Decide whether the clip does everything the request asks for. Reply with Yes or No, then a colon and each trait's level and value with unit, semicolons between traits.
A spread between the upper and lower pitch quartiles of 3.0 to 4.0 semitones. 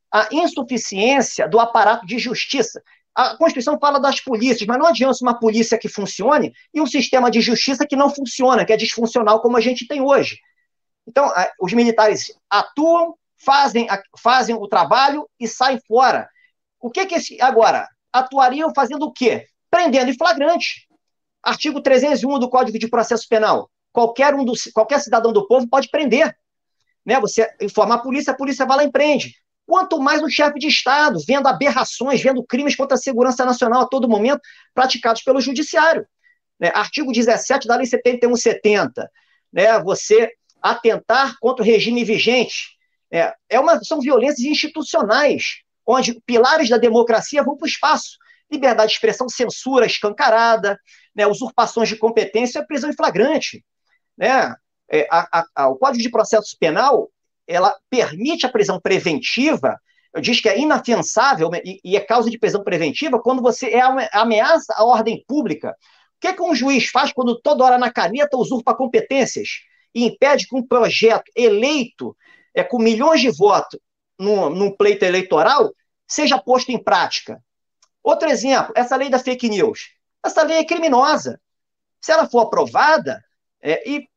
No: average, 4.5 semitones